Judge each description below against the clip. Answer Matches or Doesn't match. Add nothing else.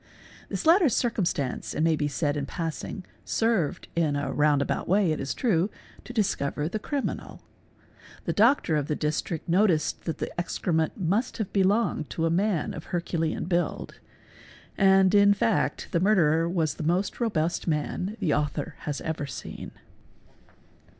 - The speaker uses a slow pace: Doesn't match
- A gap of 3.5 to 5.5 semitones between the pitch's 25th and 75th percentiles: Matches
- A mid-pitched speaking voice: Matches